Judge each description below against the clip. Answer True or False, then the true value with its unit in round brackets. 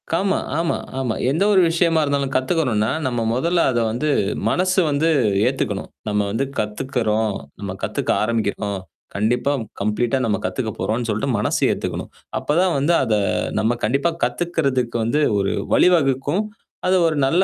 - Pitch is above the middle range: False (130 Hz)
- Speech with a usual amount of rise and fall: False (6.8 semitones)